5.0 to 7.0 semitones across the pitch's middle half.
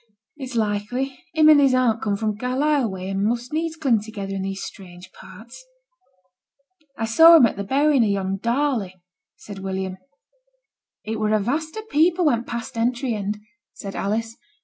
Yes: average, 5.3 semitones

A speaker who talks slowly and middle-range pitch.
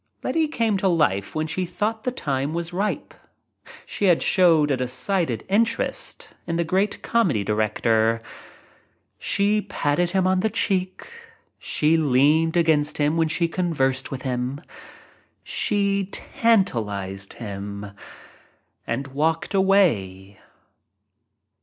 Yes: slow, 130 wpm; medium, 160 Hz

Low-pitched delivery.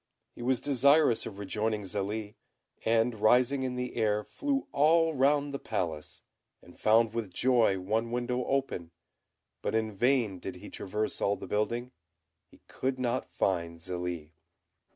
Yes: low, 115 Hz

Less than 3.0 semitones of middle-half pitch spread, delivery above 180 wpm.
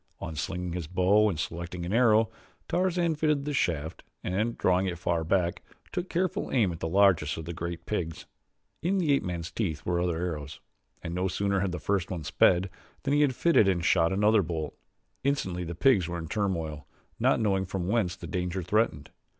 No: average, 4.0 semitones; average, 200 wpm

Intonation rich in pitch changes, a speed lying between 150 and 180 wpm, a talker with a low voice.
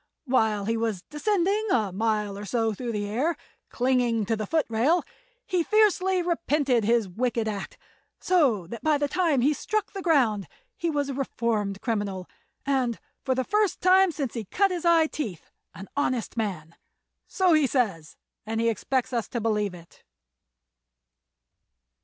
No: wide, 6.8 semitones; average, 160 wpm; high, 245 Hz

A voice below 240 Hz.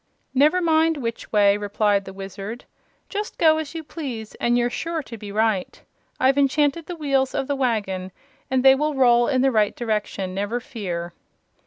No: high, 245 Hz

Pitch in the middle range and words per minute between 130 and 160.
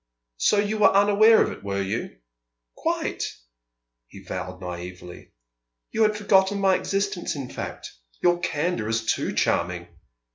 Yes: medium, 175 Hz; average, 140 wpm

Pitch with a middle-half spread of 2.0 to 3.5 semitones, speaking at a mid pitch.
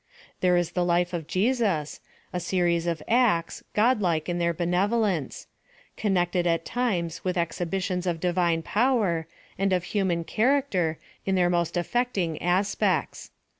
Yes: average, 2.8 semitones; medium, 180 Hz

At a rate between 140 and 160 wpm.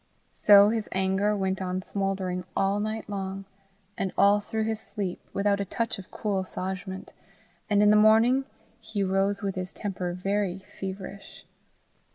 Yes: average, 155 wpm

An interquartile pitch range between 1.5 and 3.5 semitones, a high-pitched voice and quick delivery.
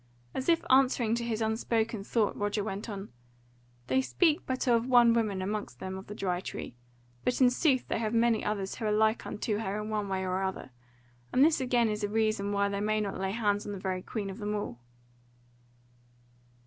Yes: average, 2.8 semitones; high, 210 Hz; fast, 210 wpm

